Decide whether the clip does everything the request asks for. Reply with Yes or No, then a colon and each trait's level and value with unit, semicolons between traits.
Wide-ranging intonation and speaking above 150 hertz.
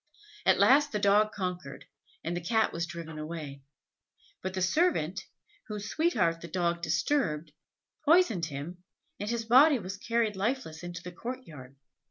Yes: wide, 5.7 semitones; medium, 185 Hz